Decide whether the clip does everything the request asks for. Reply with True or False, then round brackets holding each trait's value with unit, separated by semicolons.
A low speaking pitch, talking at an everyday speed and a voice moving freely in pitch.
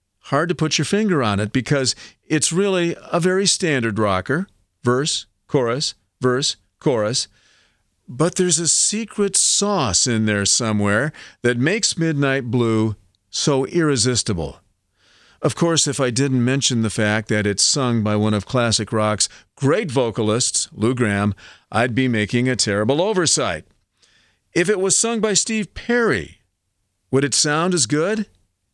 True (125 Hz; 145 wpm; 7.2 semitones)